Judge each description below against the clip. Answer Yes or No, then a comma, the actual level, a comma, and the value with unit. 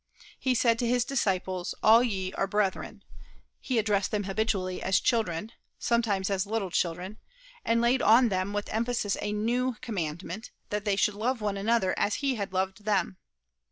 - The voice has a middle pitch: No, high, 210 Hz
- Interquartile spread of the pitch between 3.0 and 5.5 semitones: Yes, average, 3.4 semitones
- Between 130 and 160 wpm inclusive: No, average, 170 wpm